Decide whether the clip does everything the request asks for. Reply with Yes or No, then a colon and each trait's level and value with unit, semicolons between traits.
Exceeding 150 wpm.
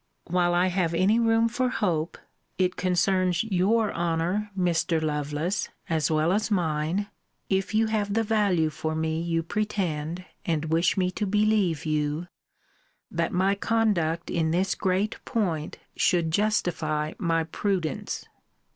No: average, 140 wpm